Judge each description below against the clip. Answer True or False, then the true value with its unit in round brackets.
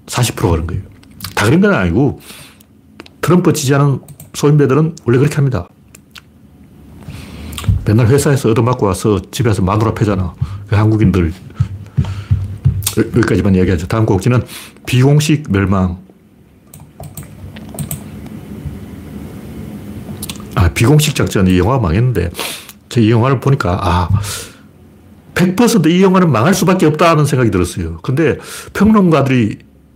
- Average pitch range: False (6.9 semitones)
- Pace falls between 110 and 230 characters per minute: False (255 characters per minute)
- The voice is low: True (110 Hz)